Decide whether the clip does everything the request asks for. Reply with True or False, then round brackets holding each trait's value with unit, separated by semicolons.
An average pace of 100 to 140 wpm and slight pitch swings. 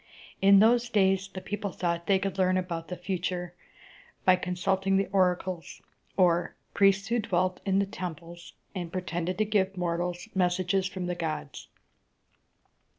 False (150 wpm; 1.7 semitones)